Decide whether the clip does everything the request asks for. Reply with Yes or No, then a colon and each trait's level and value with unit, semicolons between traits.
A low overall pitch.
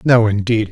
Yes: low, 110 Hz